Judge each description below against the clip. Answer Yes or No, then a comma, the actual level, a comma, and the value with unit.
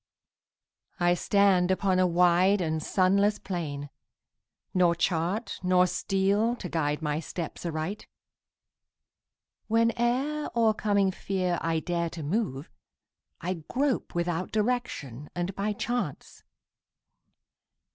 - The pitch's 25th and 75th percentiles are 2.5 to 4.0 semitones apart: Yes, average, 3.5 semitones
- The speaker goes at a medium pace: No, slow, 105 wpm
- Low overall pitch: No, medium, 185 Hz